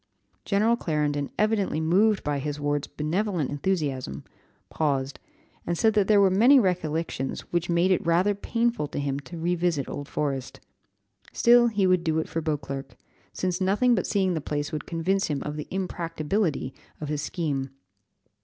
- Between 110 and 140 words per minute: No, average, 165 wpm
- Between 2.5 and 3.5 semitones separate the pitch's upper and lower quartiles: No, average, 4.7 semitones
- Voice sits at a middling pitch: Yes, medium, 165 Hz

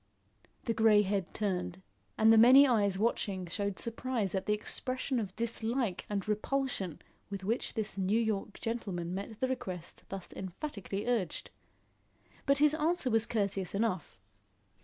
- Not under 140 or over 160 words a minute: Yes, average, 145 wpm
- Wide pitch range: No, average, 3.4 semitones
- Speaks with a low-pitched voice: No, high, 210 Hz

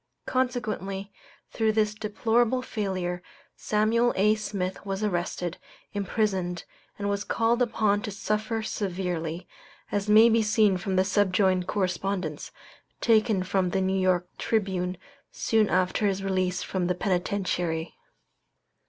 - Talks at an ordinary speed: No, slow, 125 wpm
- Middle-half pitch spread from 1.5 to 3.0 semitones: Yes, average, 2.7 semitones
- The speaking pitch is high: Yes, high, 200 Hz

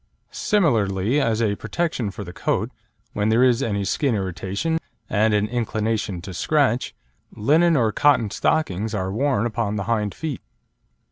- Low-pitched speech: Yes, low, 110 Hz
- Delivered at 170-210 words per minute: No, average, 150 wpm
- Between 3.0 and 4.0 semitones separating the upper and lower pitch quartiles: No, average, 5.0 semitones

